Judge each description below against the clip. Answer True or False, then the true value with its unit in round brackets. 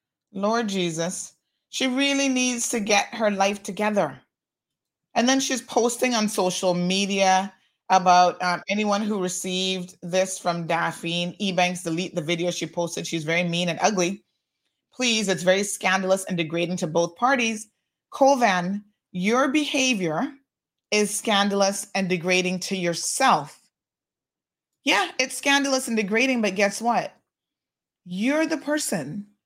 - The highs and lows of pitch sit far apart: False (4.6 semitones)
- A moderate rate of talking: False (130 wpm)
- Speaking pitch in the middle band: False (195 Hz)